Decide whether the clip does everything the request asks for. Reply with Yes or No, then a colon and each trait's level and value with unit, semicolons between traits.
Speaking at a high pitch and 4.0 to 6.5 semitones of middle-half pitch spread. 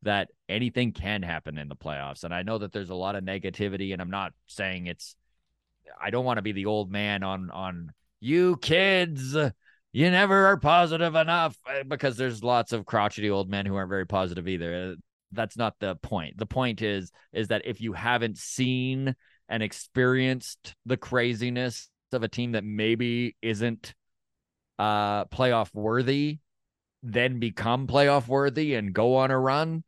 No: low, 115 Hz; average, 4.8 semitones